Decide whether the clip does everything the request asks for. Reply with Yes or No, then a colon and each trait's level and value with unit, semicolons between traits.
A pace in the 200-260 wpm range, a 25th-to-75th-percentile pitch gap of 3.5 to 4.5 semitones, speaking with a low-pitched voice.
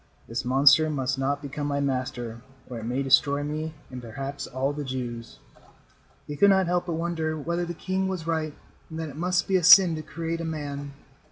No: fast, 205 wpm; average, 3.8 semitones; medium, 145 Hz